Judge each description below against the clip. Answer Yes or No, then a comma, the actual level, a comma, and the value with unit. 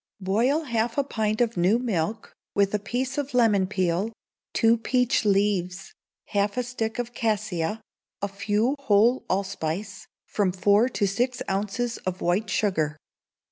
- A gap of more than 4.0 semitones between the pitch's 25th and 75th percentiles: No, average, 3.5 semitones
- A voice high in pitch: Yes, high, 210 Hz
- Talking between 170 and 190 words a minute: No, average, 145 wpm